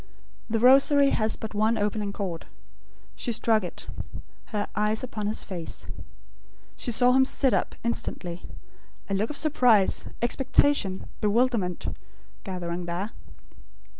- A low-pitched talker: No, high, 215 Hz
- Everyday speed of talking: No, slow, 125 wpm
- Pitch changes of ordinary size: Yes, average, 4.1 semitones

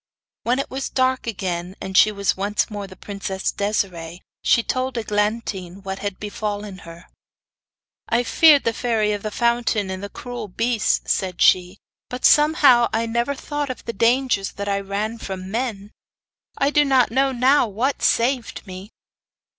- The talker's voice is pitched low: No, high, 215 Hz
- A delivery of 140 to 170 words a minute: Yes, average, 165 wpm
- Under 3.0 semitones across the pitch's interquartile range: No, average, 4.0 semitones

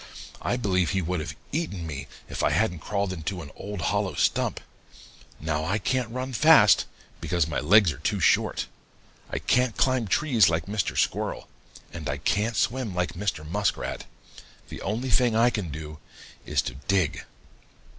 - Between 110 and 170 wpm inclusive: Yes, average, 165 wpm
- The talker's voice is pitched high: No, low, 100 Hz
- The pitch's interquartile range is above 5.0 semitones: Yes, wide, 5.6 semitones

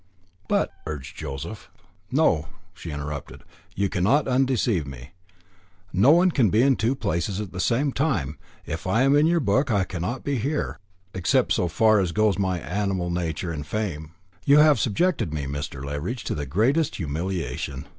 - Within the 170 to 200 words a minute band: Yes, average, 175 wpm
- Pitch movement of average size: No, wide, 8.5 semitones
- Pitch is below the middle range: Yes, very low, 95 Hz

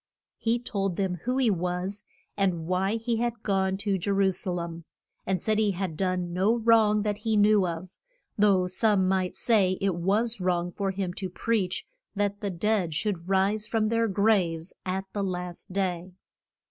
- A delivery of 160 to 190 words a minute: Yes, average, 180 wpm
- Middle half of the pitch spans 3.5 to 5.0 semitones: No, average, 2.8 semitones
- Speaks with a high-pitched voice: Yes, high, 195 Hz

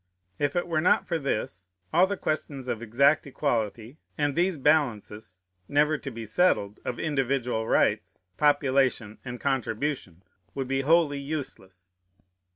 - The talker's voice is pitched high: No, low, 135 Hz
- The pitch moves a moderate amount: Yes, average, 4.9 semitones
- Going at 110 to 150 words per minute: Yes, average, 140 wpm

